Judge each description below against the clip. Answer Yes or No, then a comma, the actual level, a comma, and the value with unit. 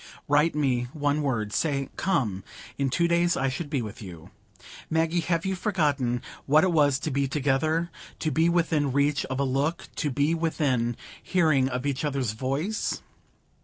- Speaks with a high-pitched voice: No, medium, 145 Hz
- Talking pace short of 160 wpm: No, average, 165 wpm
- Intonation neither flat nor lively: Yes, average, 3.6 semitones